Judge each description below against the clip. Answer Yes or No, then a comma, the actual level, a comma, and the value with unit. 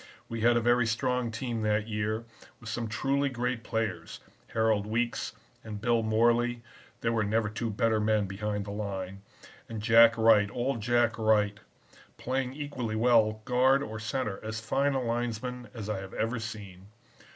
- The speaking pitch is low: Yes, low, 115 Hz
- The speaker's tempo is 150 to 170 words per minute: Yes, average, 165 wpm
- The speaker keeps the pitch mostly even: Yes, narrow, 2.1 semitones